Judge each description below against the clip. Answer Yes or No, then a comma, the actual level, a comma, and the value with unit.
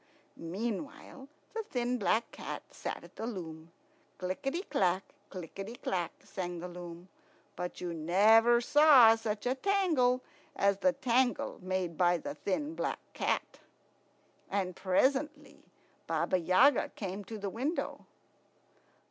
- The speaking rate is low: Yes, slow, 125 wpm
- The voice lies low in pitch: No, high, 210 Hz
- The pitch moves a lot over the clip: Yes, wide, 6.1 semitones